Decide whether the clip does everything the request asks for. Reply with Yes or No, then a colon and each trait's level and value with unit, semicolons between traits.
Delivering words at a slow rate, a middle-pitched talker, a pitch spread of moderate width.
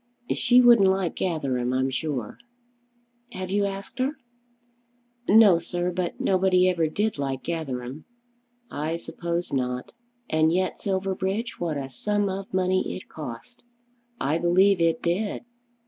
Yes: slow, 130 wpm; medium, 175 Hz; average, 4.1 semitones